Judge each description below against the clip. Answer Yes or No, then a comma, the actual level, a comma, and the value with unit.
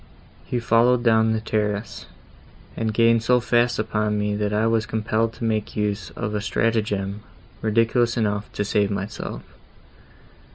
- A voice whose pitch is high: No, low, 110 Hz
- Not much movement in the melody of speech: Yes, narrow, 1.6 semitones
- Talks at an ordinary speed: Yes, average, 150 wpm